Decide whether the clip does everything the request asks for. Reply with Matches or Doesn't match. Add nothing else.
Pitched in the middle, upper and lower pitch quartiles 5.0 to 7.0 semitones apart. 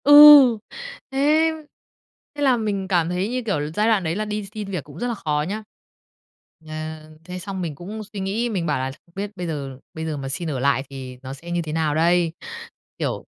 Matches